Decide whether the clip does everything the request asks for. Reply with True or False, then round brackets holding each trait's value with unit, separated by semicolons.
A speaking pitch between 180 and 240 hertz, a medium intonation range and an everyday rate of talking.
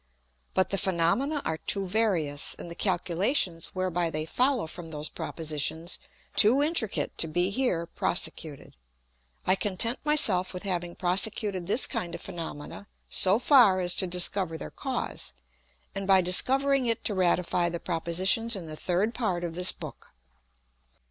True (185 Hz; 3.9 semitones; 155 wpm)